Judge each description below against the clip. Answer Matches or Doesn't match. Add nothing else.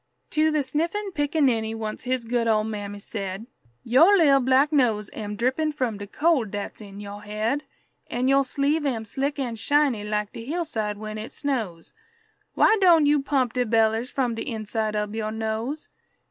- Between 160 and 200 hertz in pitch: Doesn't match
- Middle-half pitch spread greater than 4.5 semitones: Matches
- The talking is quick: Doesn't match